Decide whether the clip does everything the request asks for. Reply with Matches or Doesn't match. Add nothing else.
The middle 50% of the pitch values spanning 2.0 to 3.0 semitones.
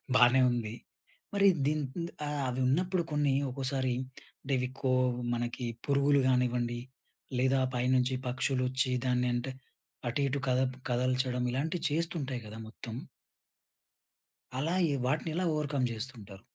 Matches